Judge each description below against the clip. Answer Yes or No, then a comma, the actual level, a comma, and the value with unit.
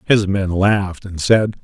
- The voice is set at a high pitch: No, low, 100 Hz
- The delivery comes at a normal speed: Yes, average, 185 wpm